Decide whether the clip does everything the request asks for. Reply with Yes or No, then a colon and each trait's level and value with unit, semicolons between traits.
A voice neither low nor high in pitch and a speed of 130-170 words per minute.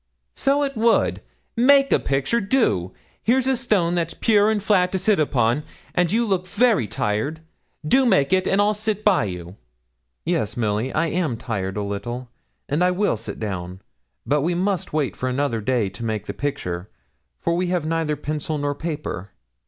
No: medium, 160 Hz; average, 185 wpm